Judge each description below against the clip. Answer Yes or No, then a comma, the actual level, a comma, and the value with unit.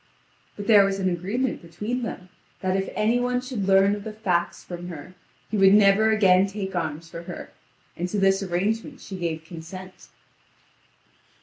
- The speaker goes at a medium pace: Yes, average, 175 wpm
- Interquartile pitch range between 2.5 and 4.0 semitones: Yes, average, 3.2 semitones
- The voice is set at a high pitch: Yes, high, 195 Hz